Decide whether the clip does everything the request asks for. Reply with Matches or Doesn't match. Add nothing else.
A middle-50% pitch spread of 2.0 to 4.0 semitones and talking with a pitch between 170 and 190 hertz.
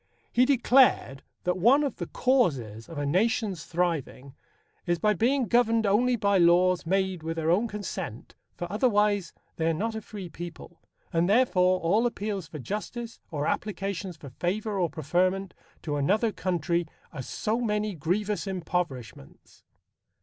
Doesn't match